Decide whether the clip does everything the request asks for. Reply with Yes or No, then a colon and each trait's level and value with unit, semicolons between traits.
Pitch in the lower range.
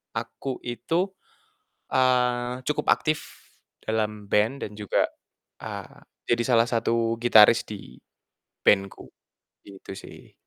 Yes: low, 115 Hz